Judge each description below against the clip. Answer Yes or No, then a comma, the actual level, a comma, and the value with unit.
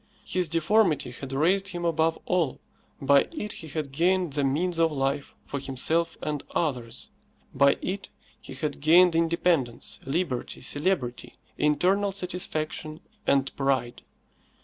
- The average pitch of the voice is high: No, medium, 155 Hz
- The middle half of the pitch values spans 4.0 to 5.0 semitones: Yes, average, 4.4 semitones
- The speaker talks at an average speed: No, slow, 130 wpm